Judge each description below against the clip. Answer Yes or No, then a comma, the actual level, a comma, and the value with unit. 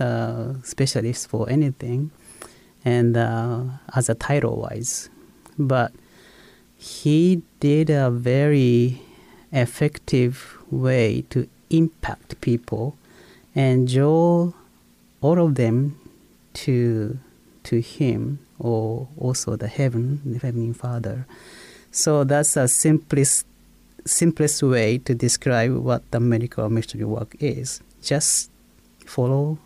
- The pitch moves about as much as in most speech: Yes, average, 3.8 semitones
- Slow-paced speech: Yes, slow, 100 wpm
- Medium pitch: No, low, 125 Hz